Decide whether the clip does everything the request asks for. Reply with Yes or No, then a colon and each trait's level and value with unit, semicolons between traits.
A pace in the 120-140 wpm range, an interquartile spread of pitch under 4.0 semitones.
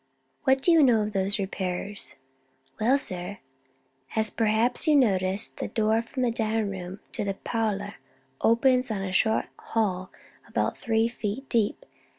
No: average, 160 wpm; average, 3.0 semitones